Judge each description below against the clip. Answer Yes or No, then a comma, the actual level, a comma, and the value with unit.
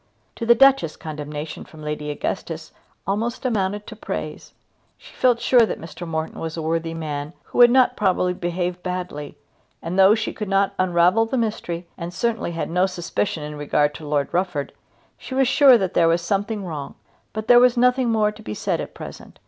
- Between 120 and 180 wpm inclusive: No, average, 195 wpm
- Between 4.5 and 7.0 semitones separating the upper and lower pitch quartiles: Yes, wide, 5.6 semitones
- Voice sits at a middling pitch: Yes, medium, 180 Hz